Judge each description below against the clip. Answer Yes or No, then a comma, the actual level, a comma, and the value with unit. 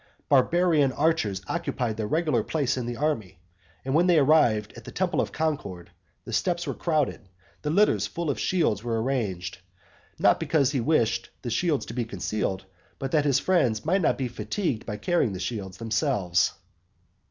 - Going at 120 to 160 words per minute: No, average, 175 wpm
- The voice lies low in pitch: Yes, low, 130 Hz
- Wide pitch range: Yes, wide, 6.6 semitones